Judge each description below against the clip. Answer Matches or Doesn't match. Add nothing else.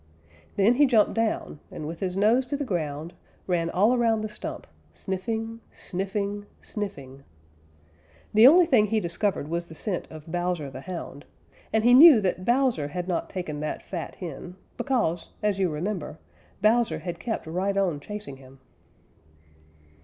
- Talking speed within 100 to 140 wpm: Doesn't match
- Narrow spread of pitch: Doesn't match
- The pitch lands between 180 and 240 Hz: Matches